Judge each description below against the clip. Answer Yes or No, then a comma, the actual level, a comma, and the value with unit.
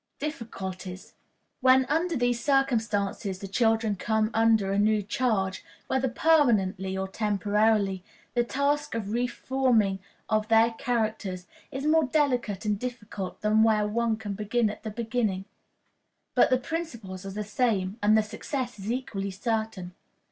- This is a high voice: Yes, high, 220 Hz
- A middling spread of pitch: Yes, average, 3.7 semitones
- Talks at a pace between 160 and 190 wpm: No, average, 150 wpm